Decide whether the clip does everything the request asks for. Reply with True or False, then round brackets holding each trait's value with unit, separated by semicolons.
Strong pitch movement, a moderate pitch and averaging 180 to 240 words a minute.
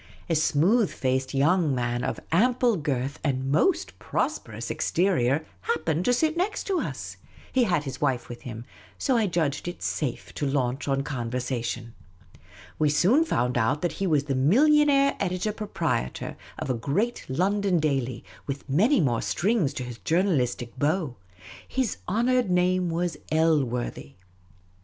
False (7.3 semitones; 155 Hz; 150 wpm)